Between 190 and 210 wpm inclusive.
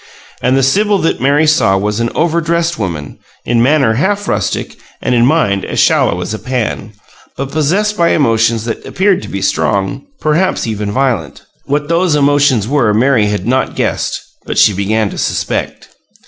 No: average, 175 wpm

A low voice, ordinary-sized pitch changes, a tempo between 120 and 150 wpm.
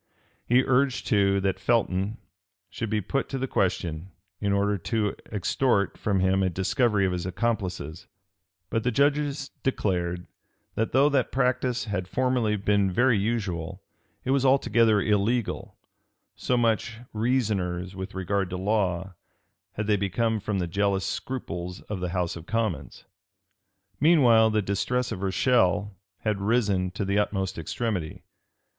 Yes: low, 105 Hz; average, 4.0 semitones; average, 145 wpm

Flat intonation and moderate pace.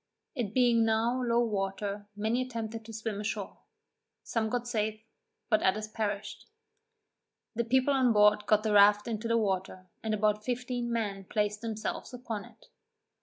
Yes: narrow, 2.2 semitones; average, 155 wpm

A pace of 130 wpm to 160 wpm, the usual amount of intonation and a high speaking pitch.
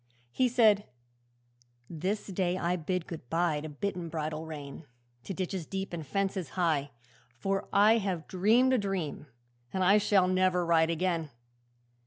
No: average, 155 wpm; average, 3.4 semitones; medium, 180 Hz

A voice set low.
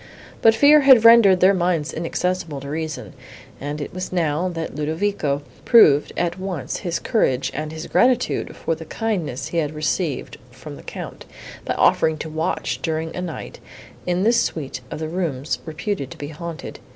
No: medium, 165 Hz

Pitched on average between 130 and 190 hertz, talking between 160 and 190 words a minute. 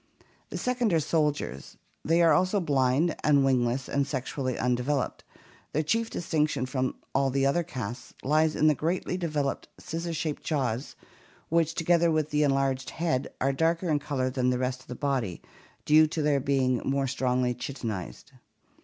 Yes: medium, 140 Hz; average, 170 wpm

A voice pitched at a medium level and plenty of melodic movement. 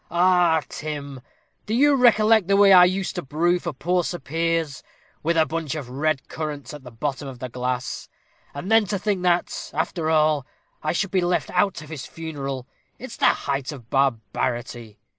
No: medium, 160 Hz; average, 4.6 semitones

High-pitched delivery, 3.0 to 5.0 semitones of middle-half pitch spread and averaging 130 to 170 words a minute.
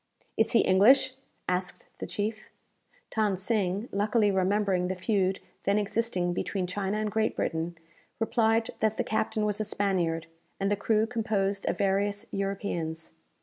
No: high, 200 Hz; narrow, 2.5 semitones; average, 150 wpm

